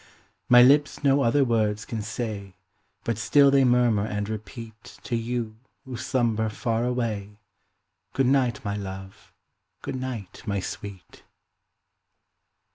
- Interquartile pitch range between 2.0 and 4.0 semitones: Yes, average, 3.2 semitones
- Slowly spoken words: Yes, slow, 125 wpm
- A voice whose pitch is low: Yes, low, 115 Hz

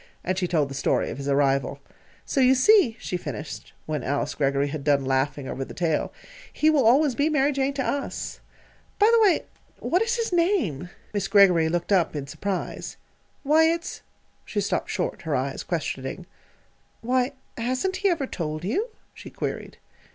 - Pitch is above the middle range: Yes, high, 205 Hz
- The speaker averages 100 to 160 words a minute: No, average, 180 wpm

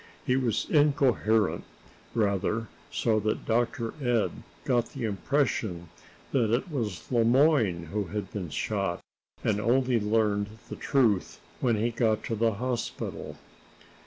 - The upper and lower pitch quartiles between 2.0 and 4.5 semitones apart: Yes, average, 2.9 semitones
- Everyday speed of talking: No, slow, 130 wpm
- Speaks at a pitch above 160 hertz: No, low, 115 Hz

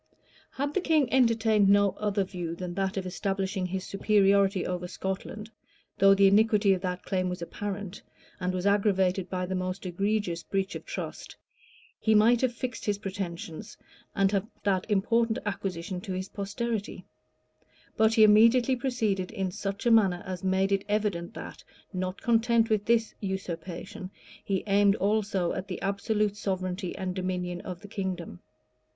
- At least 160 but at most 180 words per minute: Yes, average, 165 wpm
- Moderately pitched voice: No, high, 195 Hz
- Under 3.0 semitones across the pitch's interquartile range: Yes, narrow, 2.4 semitones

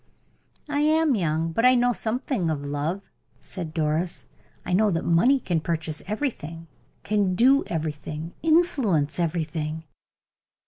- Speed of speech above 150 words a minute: No, slow, 135 wpm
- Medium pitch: Yes, medium, 175 Hz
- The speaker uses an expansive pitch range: Yes, wide, 7.4 semitones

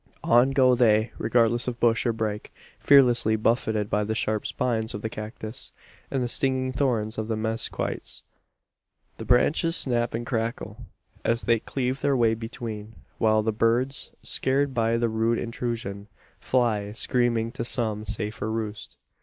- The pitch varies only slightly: Yes, narrow, 2.1 semitones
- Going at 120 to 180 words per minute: Yes, average, 155 wpm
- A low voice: Yes, low, 115 Hz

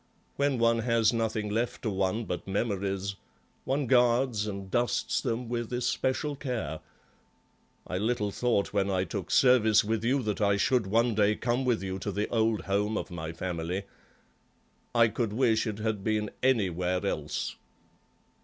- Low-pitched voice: Yes, low, 110 Hz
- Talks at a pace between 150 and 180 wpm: Yes, average, 160 wpm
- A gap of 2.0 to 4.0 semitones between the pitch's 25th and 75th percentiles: Yes, average, 3.4 semitones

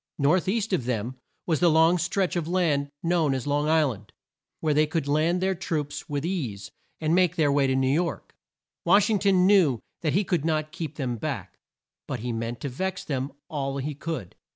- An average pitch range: Yes, average, 4.4 semitones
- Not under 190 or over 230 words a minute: Yes, fast, 205 wpm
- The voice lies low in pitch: No, medium, 155 Hz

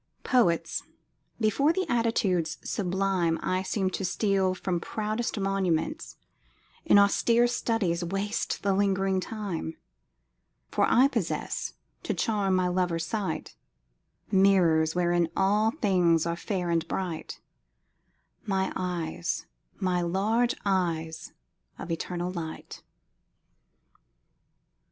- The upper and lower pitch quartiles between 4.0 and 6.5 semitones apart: No, average, 3.3 semitones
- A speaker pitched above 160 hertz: Yes, high, 190 Hz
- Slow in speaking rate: Yes, slow, 105 wpm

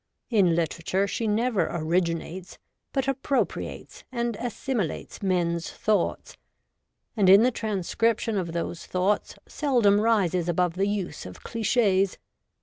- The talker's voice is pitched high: Yes, high, 195 Hz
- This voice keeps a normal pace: No, slow, 125 wpm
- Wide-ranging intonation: No, average, 4.6 semitones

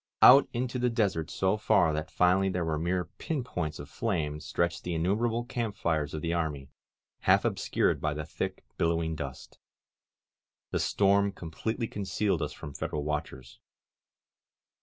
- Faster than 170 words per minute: No, average, 155 wpm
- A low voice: Yes, very low, 90 Hz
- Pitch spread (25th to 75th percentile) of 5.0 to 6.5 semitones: Yes, average, 5.3 semitones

